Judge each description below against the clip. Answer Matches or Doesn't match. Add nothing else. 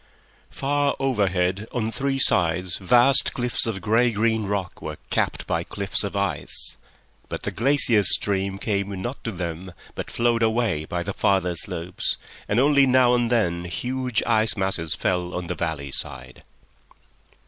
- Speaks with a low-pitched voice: Matches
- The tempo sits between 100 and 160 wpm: Matches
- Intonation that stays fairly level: Doesn't match